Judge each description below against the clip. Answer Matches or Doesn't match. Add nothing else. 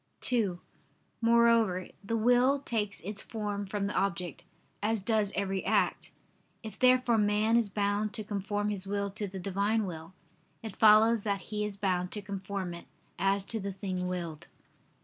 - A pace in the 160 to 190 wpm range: Matches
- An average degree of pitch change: Doesn't match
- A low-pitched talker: Doesn't match